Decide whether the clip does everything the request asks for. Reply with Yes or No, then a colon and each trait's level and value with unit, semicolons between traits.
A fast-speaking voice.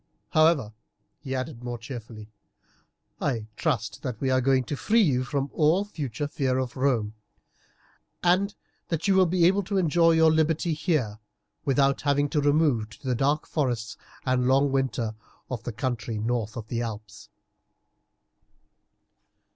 No: average, 150 wpm